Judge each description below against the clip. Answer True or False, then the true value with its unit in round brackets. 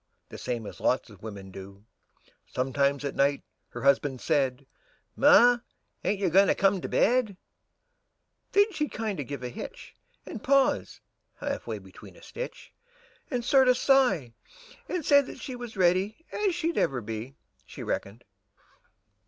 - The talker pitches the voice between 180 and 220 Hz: True (190 Hz)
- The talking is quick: False (155 wpm)